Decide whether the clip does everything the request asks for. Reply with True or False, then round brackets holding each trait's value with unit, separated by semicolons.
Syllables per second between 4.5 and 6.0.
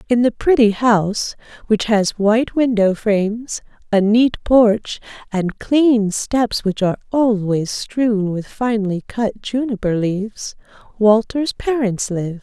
False (3.8 syllables/s)